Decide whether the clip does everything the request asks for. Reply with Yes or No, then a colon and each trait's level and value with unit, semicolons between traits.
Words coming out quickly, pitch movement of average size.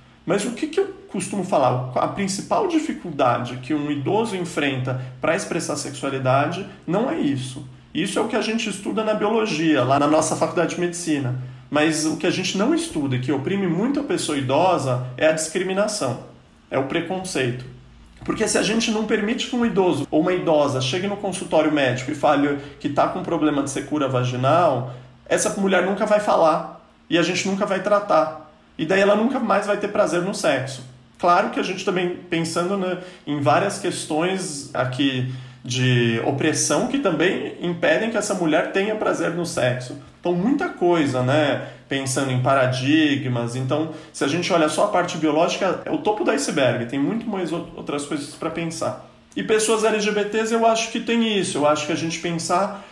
No: fast, 190 wpm; wide, 5.9 semitones